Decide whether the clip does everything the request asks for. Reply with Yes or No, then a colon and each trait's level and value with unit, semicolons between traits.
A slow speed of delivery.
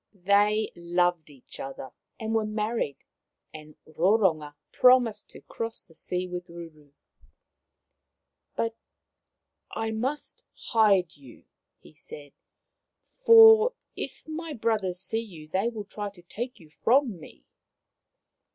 Yes: slow, 125 wpm